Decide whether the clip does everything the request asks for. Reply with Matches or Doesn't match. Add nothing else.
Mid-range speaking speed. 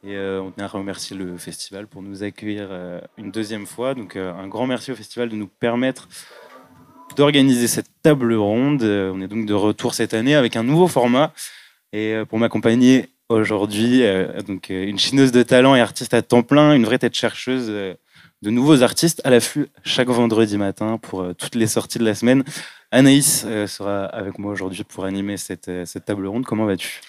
Matches